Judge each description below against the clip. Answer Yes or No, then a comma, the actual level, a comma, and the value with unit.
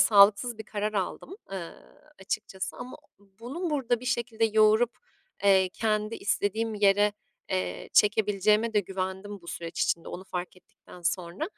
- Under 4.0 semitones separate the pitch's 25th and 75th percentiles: Yes, average, 2.9 semitones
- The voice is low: No, high, 210 Hz